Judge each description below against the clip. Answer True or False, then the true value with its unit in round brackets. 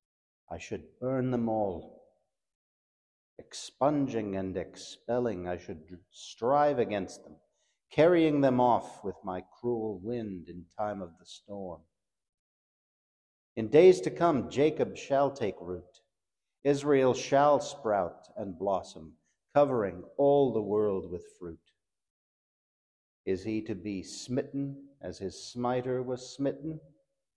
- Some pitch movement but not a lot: False (7.0 semitones)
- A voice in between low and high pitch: False (110 Hz)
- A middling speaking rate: False (120 wpm)